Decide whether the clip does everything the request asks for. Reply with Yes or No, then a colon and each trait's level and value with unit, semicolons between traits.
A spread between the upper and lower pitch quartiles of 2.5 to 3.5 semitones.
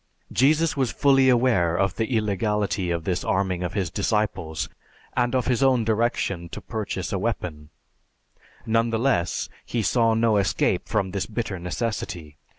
No: average, 4.6 semitones